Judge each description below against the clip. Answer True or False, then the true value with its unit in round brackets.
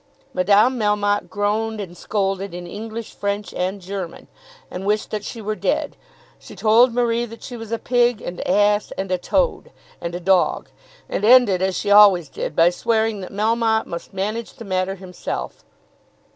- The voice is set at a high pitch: True (205 Hz)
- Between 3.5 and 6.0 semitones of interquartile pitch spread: False (3.0 semitones)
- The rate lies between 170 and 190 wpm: True (175 wpm)